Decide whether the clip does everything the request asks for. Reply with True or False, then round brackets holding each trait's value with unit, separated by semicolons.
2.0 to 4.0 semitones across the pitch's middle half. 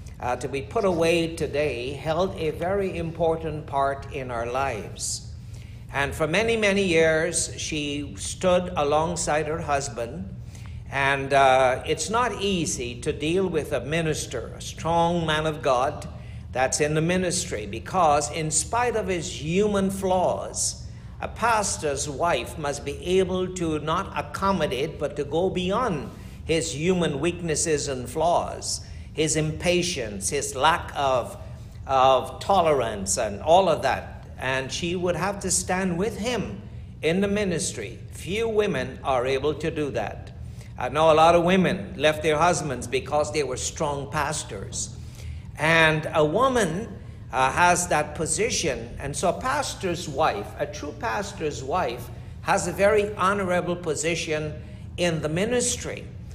False (5.2 semitones)